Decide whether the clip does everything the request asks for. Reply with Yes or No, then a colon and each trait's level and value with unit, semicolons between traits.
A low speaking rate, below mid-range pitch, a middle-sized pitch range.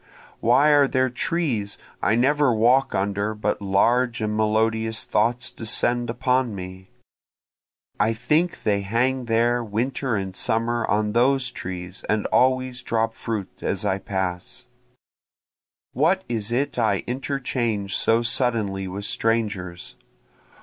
Yes: slow, 125 wpm; low, 115 Hz; average, 3.7 semitones